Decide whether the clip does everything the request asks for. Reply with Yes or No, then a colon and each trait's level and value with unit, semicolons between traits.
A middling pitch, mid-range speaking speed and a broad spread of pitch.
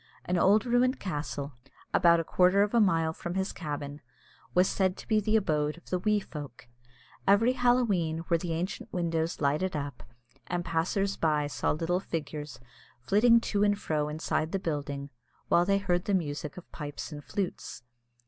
No: medium, 175 Hz; average, 175 wpm; average, 4.7 semitones